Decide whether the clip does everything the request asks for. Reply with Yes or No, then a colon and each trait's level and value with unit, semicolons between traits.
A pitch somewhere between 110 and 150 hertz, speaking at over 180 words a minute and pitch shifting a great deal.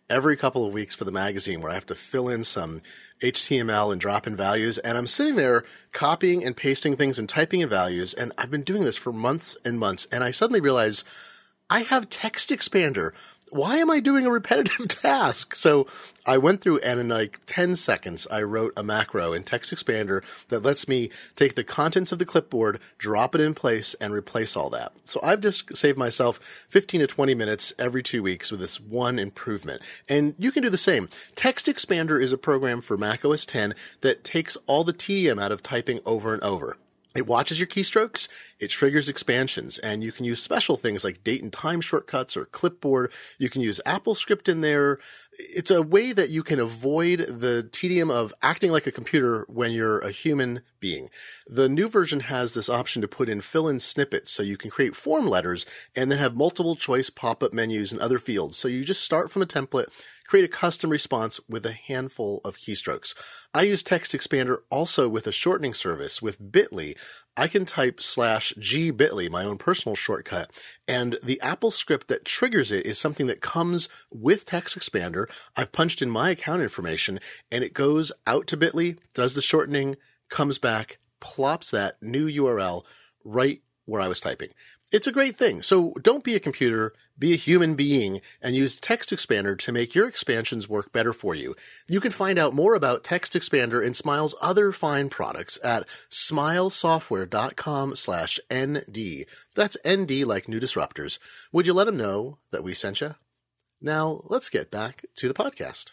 Yes: medium, 140 Hz; average, 195 wpm; wide, 7.5 semitones